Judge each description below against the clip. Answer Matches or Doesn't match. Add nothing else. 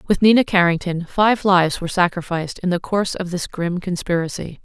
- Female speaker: Matches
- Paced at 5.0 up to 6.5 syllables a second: Matches